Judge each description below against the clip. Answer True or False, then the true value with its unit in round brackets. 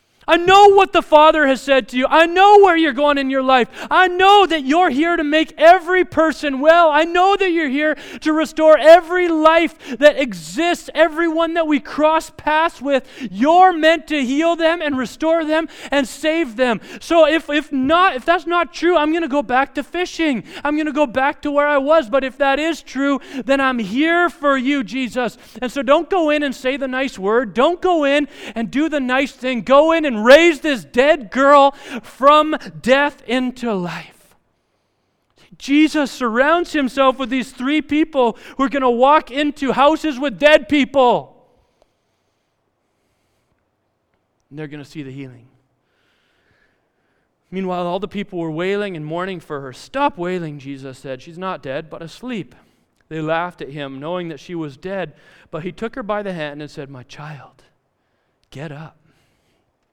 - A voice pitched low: False (280 Hz)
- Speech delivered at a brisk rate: True (185 wpm)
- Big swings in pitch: True (6.0 semitones)